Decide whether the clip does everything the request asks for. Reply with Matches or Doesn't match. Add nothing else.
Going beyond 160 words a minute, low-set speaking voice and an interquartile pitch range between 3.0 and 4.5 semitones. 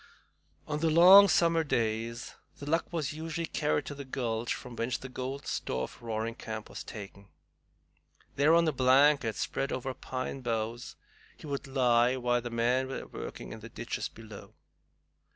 Matches